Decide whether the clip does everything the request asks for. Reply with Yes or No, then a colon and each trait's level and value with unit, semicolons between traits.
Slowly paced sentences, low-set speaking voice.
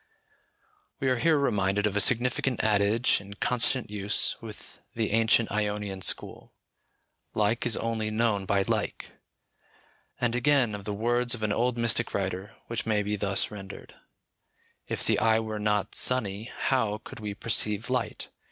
No: average, 155 wpm; low, 110 Hz